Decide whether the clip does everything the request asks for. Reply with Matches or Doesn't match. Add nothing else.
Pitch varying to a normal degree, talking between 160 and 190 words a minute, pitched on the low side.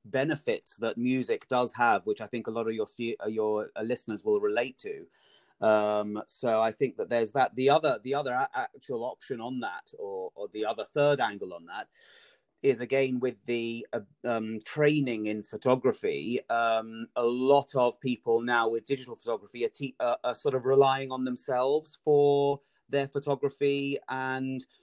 Matches